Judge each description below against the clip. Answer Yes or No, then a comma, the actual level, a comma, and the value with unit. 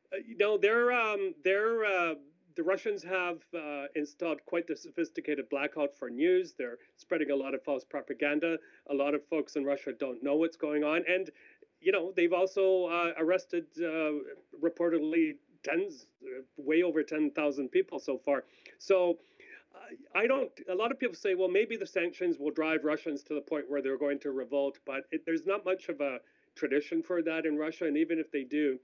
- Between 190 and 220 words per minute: Yes, average, 200 wpm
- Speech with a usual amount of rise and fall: Yes, average, 4.6 semitones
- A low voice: No, medium, 165 Hz